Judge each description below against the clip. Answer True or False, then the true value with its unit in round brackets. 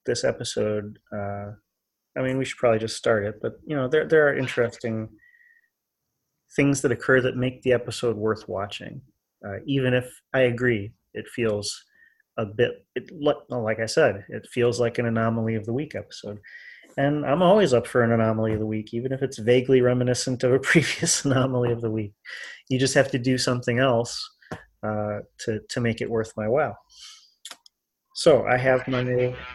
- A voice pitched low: True (125 Hz)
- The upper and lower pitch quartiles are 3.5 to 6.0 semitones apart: False (2.9 semitones)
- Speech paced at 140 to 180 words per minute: False (190 wpm)